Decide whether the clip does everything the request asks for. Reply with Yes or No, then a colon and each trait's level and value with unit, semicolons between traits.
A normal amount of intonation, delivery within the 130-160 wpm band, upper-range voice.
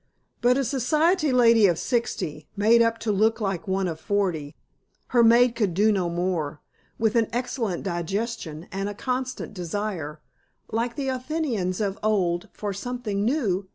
Yes: average, 4.6 semitones; average, 155 wpm; high, 210 Hz